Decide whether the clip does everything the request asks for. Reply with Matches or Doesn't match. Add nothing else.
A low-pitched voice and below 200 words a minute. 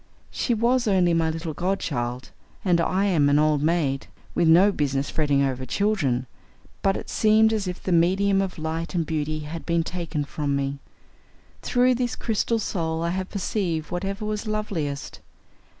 Doesn't match